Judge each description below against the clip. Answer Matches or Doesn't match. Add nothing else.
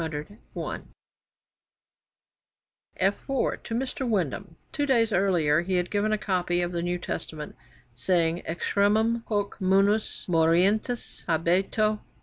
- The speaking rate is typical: Doesn't match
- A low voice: Doesn't match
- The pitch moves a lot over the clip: Doesn't match